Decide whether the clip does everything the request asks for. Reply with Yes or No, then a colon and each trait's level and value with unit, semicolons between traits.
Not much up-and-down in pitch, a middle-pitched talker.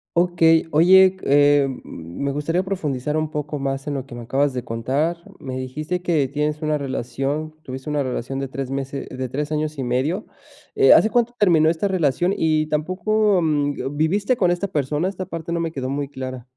No: average, 3.9 semitones; medium, 150 Hz